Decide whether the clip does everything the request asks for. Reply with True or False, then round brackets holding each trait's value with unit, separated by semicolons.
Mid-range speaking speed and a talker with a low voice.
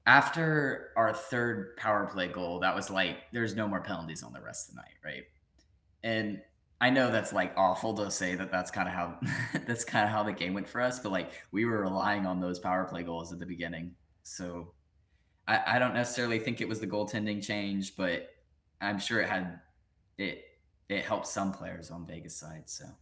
False (210 wpm; 95 Hz)